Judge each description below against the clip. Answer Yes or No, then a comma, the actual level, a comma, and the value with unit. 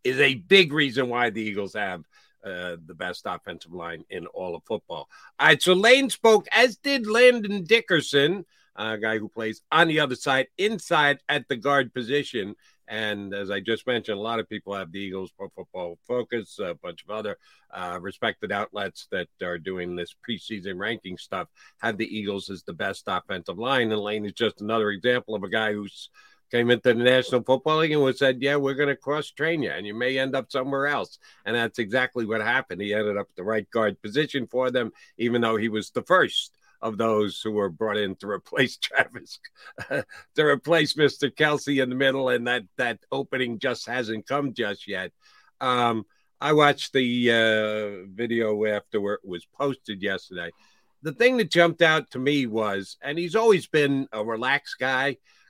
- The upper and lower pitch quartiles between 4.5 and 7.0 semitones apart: Yes, average, 5.2 semitones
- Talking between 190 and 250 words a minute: Yes, average, 195 wpm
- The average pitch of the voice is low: Yes, low, 120 Hz